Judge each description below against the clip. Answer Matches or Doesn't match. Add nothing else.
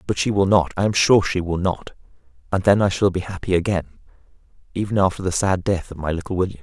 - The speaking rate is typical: Doesn't match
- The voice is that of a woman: Doesn't match